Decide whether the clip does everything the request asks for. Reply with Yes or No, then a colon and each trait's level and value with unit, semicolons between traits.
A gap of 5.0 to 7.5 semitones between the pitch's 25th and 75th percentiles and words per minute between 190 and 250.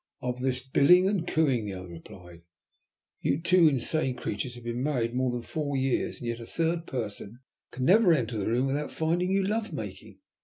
Yes: wide, 5.6 semitones; average, 195 wpm